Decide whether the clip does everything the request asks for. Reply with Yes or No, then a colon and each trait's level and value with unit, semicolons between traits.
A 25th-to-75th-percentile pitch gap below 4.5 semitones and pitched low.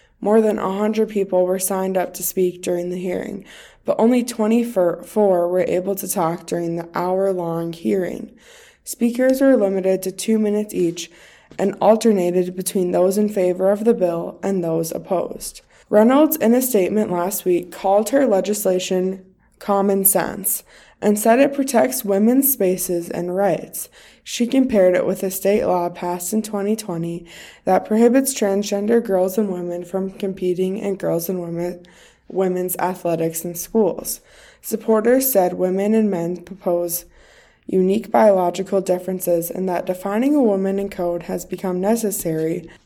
No: average, 3.1 semitones; high, 190 Hz